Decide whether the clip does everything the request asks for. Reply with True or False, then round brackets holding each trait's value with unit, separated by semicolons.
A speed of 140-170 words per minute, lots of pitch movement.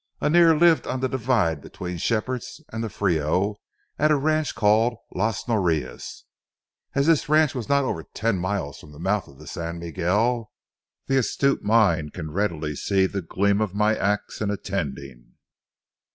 True (165 wpm; 6.6 semitones)